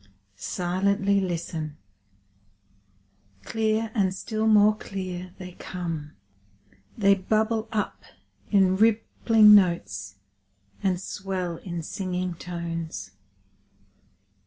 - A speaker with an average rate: No, slow, 85 wpm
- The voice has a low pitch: No, medium, 185 Hz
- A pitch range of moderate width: Yes, average, 3.3 semitones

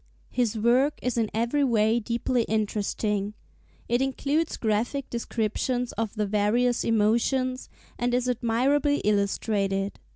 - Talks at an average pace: No, slow, 120 wpm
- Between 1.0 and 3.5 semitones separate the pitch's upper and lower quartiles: Yes, average, 2.9 semitones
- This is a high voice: Yes, high, 235 Hz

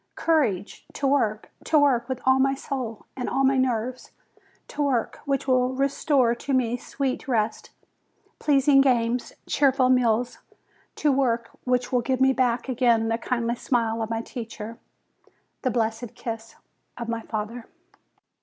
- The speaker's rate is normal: Yes, average, 150 wpm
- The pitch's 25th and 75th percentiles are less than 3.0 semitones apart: Yes, narrow, 2.6 semitones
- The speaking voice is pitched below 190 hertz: No, very high, 250 Hz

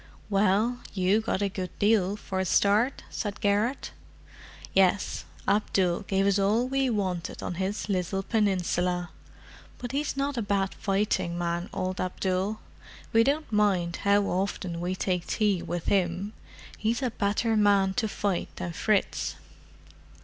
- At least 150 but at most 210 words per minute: No, average, 140 wpm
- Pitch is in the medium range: No, high, 200 Hz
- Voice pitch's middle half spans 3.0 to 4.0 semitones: No, narrow, 2.6 semitones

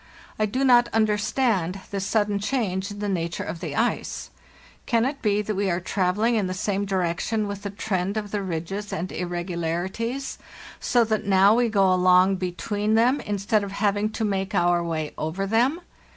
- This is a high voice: Yes, high, 200 Hz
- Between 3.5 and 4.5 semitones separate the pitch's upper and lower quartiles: No, average, 2.9 semitones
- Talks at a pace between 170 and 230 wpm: Yes, average, 185 wpm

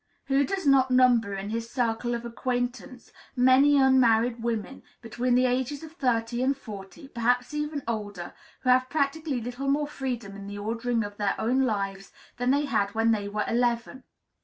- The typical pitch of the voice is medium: No, high, 245 Hz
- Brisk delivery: No, average, 175 wpm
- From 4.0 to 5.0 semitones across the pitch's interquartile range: No, average, 3.0 semitones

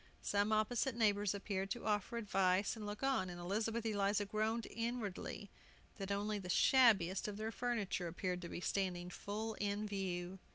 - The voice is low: No, high, 205 Hz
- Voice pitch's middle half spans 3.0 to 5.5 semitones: No, narrow, 2.5 semitones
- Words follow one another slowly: No, average, 165 wpm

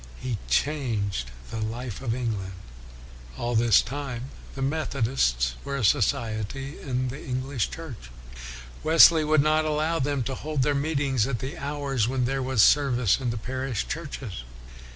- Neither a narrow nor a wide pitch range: Yes, average, 3.7 semitones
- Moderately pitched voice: No, low, 130 Hz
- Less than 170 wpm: Yes, average, 155 wpm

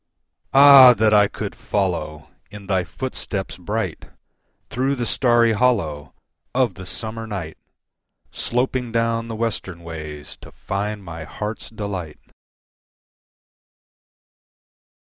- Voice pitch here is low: Yes, low, 105 Hz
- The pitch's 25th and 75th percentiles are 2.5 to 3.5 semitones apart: No, average, 4.6 semitones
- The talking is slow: Yes, slow, 105 wpm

